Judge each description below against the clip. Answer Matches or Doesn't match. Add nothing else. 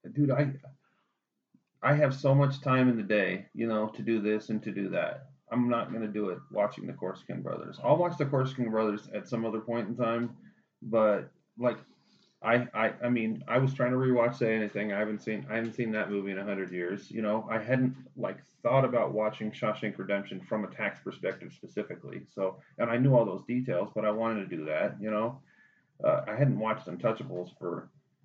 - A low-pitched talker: Matches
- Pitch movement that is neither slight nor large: Matches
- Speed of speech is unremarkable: Doesn't match